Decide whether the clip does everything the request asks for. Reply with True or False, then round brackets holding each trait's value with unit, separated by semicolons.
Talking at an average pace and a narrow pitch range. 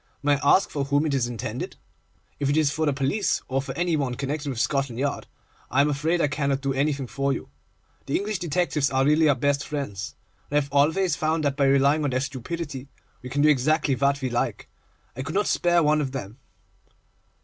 False (220 wpm; 2.1 semitones)